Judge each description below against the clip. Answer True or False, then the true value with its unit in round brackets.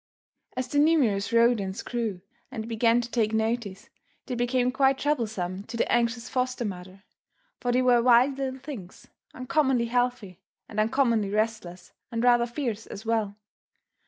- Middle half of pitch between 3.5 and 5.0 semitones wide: False (2.9 semitones)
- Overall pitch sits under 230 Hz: False (235 Hz)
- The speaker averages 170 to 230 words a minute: False (150 wpm)